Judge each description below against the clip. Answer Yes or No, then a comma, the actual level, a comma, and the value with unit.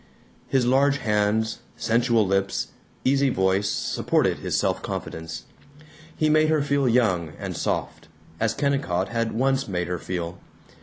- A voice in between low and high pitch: No, low, 115 Hz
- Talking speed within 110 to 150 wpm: Yes, average, 140 wpm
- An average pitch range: No, wide, 6.2 semitones